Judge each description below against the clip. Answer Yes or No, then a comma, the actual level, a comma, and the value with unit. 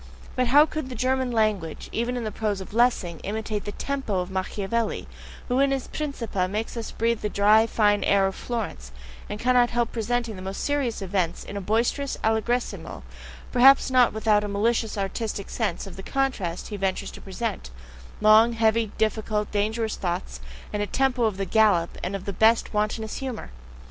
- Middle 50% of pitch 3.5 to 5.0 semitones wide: No, average, 3.1 semitones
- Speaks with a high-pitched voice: Yes, high, 220 Hz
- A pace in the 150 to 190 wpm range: Yes, average, 185 wpm